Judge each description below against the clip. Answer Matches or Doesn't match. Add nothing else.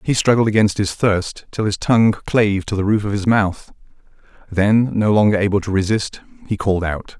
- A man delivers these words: Matches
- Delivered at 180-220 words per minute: Matches